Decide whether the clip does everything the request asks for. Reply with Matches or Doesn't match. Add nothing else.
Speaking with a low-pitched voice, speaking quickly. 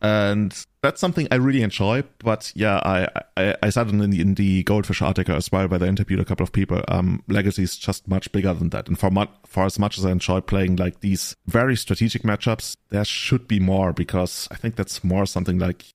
Matches